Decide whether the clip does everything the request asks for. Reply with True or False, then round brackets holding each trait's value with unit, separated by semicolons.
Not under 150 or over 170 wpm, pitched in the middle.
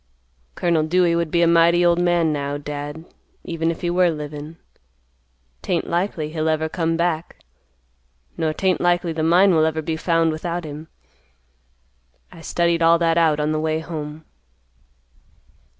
True (155 wpm; 165 Hz)